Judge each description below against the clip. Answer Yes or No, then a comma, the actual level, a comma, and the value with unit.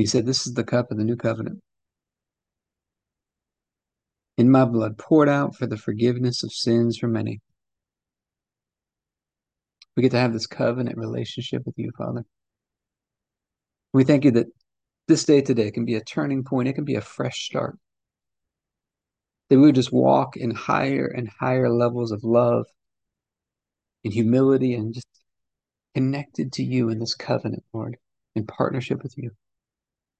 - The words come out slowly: No, average, 155 wpm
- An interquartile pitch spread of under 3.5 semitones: Yes, average, 2.9 semitones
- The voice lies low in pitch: Yes, low, 120 Hz